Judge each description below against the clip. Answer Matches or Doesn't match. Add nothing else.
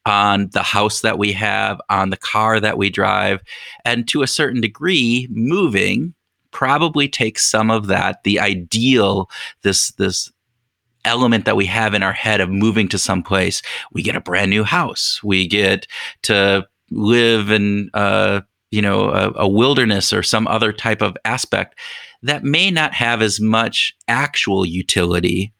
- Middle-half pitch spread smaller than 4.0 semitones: Matches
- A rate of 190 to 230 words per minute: Doesn't match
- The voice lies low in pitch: Matches